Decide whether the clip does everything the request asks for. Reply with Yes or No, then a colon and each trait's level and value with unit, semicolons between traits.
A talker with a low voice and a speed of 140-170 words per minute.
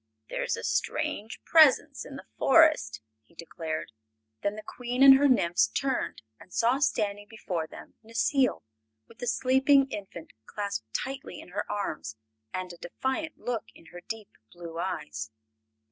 No: high, 215 Hz; average, 155 wpm